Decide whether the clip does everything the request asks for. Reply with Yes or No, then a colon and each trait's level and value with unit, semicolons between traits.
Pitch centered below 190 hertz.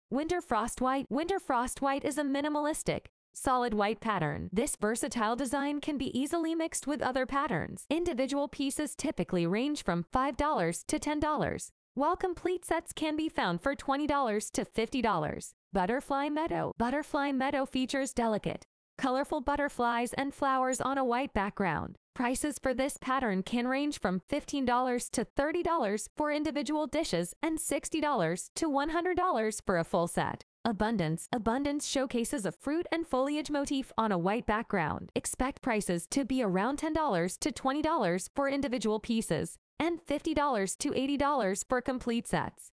No: very high, 270 Hz